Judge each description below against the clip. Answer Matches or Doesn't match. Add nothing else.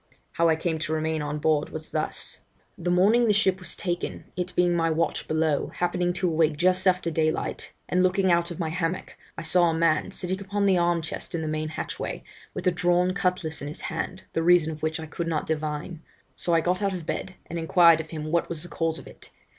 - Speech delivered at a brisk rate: Matches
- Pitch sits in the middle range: Matches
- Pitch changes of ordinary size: Doesn't match